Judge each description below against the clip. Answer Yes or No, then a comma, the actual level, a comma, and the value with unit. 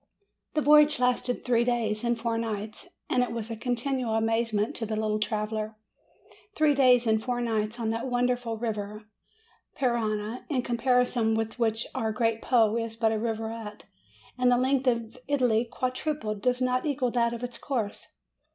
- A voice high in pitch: Yes, high, 235 Hz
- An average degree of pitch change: No, narrow, 2.1 semitones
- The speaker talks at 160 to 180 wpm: Yes, average, 170 wpm